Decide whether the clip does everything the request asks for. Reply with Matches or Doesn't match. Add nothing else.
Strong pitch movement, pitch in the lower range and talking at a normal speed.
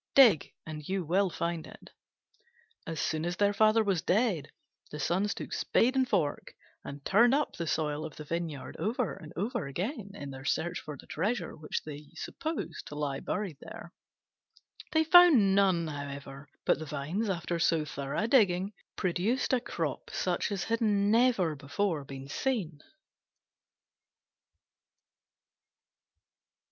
Doesn't match